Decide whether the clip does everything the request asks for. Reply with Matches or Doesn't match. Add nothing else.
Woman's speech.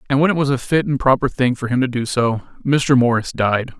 Doesn't match